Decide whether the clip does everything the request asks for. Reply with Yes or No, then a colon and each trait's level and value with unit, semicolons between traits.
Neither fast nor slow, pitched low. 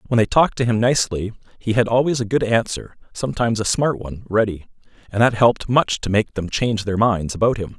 No: fast, 225 wpm; low, 115 Hz